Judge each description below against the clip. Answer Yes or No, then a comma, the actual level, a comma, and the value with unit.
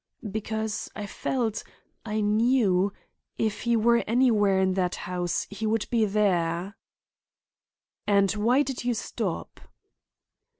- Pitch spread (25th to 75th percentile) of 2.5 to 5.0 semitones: Yes, average, 2.8 semitones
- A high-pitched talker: Yes, high, 210 Hz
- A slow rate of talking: Yes, slow, 110 wpm